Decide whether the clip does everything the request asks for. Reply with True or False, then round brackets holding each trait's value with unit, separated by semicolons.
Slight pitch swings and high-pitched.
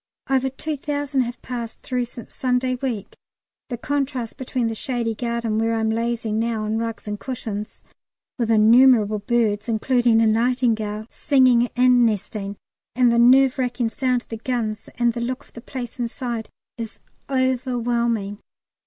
True (2.3 semitones; 235 Hz)